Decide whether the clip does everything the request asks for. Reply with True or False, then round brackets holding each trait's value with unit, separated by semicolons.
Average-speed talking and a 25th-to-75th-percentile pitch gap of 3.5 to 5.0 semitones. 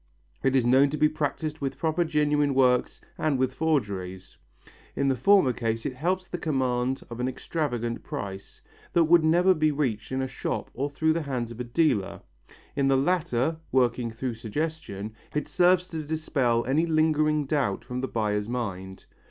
True (175 wpm; 4.7 semitones)